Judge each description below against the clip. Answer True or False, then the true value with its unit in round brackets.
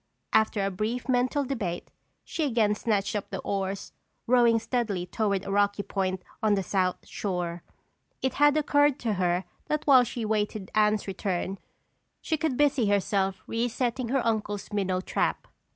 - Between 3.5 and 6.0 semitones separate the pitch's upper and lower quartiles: True (4.1 semitones)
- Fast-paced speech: False (155 wpm)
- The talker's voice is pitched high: True (210 Hz)